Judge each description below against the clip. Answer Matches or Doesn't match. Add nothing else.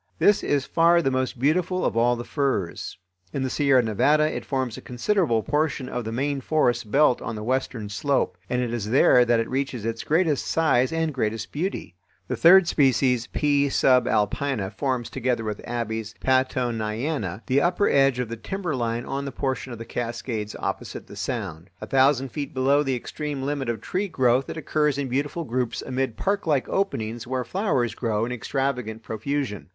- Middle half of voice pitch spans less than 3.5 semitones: Doesn't match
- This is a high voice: Doesn't match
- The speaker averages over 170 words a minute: Matches